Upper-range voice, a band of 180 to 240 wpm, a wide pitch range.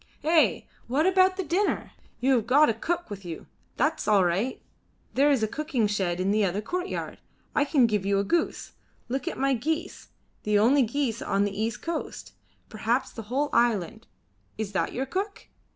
Yes: high, 240 Hz; average, 190 wpm; wide, 6.4 semitones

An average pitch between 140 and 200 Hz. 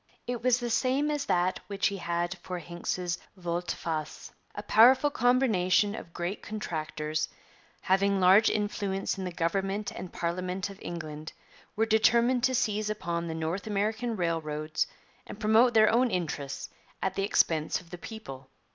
Yes: high, 190 Hz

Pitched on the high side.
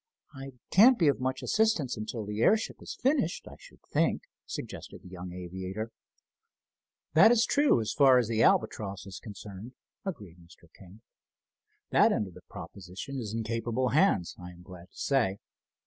No: low, 110 Hz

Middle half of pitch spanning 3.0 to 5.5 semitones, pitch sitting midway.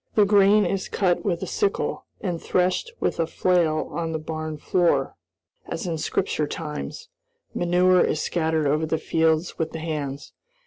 No: narrow, 2.5 semitones; medium, 165 Hz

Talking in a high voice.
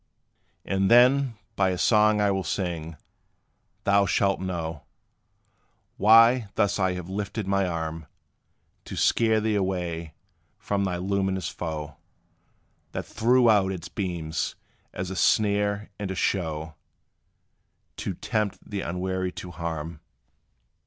No: very low, 95 Hz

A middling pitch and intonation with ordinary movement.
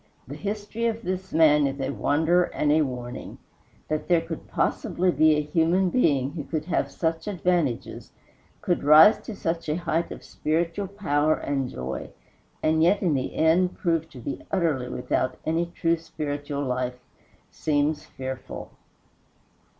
Yes: medium, 160 Hz; average, 3.4 semitones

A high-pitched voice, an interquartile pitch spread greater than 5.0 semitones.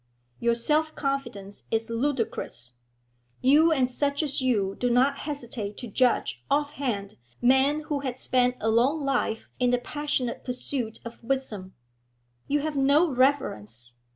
No: very high, 255 Hz; average, 3.8 semitones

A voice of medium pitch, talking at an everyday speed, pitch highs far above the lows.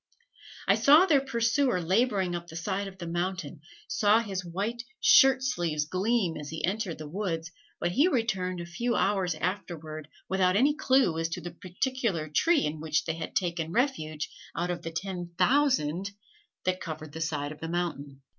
Yes: medium, 180 Hz; average, 180 wpm; wide, 5.9 semitones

